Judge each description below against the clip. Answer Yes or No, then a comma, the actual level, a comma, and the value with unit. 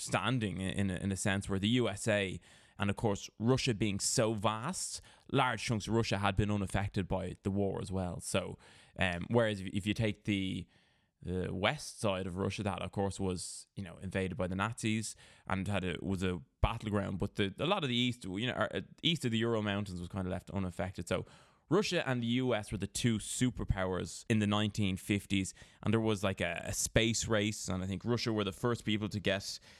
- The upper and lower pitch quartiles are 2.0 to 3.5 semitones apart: Yes, average, 2.9 semitones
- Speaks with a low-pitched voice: Yes, low, 100 Hz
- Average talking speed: No, fast, 210 wpm